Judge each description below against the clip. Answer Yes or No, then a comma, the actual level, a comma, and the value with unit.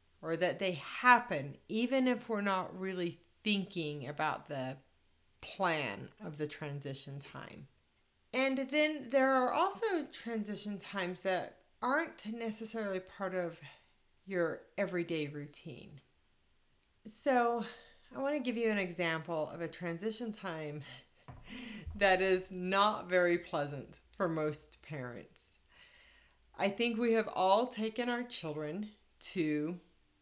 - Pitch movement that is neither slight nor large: No, wide, 6.7 semitones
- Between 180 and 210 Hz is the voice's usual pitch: Yes, high, 190 Hz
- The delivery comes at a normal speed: No, slow, 120 wpm